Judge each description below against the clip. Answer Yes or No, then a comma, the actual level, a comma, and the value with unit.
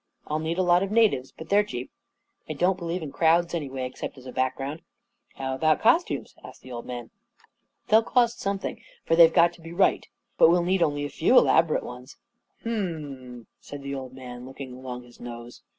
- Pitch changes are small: No, average, 5.2 semitones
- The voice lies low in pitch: No, medium, 155 Hz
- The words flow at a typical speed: No, fast, 225 wpm